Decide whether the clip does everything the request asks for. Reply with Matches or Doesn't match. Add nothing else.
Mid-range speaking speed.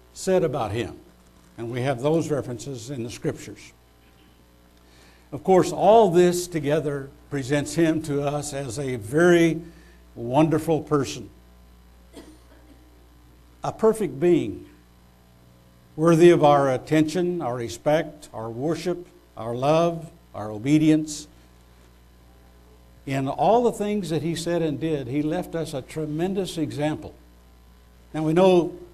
Doesn't match